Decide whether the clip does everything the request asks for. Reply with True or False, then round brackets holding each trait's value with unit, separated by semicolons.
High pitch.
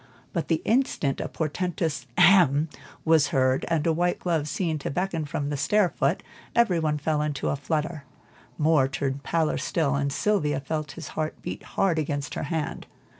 False (155 Hz)